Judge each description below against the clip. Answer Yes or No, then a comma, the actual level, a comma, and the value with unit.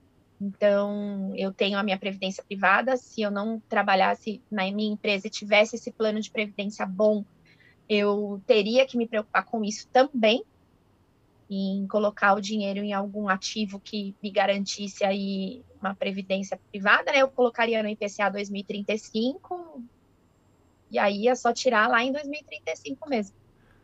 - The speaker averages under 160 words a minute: Yes, average, 145 wpm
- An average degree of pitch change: No, narrow, 2.2 semitones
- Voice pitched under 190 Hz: No, high, 205 Hz